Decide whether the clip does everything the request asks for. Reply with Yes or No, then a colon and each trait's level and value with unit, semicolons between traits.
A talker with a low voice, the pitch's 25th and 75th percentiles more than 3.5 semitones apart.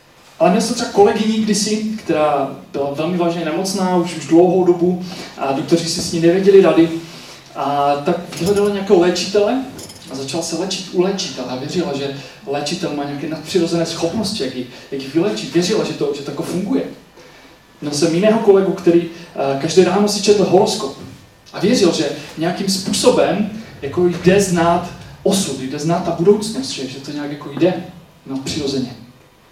No: medium, 170 Hz; average, 4.7 semitones